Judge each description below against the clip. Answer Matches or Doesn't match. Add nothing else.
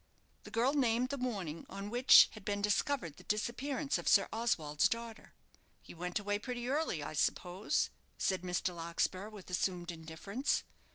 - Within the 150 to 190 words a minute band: Matches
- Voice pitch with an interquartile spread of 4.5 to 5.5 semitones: Matches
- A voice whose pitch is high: Matches